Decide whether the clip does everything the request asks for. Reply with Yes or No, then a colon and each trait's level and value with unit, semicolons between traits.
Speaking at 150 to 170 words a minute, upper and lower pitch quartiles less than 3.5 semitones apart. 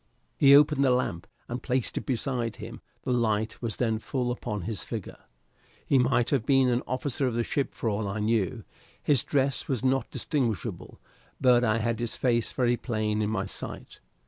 No: average, 190 wpm; average, 3.0 semitones